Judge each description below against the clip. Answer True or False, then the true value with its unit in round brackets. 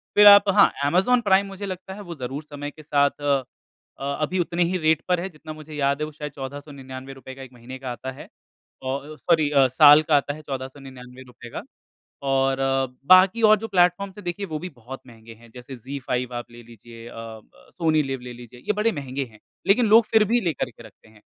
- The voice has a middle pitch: True (145 Hz)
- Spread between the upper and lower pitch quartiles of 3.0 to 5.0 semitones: False (5.4 semitones)